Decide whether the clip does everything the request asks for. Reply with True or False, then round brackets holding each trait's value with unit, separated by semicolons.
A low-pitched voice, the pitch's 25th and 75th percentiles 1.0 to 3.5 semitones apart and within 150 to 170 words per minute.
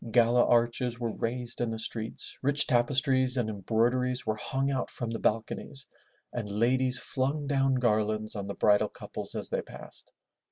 True (120 Hz; 2.7 semitones; 165 wpm)